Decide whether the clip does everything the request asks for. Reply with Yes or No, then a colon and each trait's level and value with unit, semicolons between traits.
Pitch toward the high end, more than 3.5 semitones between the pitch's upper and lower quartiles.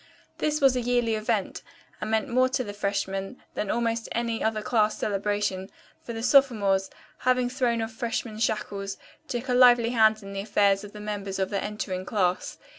No: high, 220 Hz; average, 3.0 semitones